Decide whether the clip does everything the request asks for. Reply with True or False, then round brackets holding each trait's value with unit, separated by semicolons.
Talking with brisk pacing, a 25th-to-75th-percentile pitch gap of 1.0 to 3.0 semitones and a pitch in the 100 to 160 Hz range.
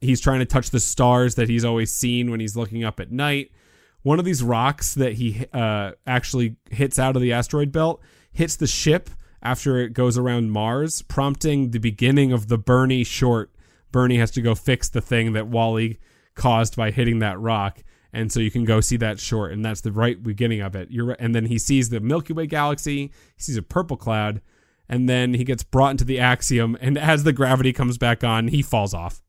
True (220 wpm; 2.7 semitones; 120 Hz)